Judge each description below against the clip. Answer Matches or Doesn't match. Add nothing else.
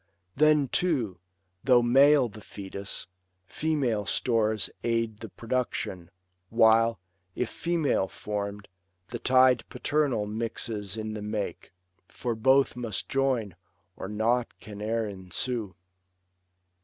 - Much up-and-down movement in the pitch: Doesn't match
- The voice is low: Matches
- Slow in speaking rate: Matches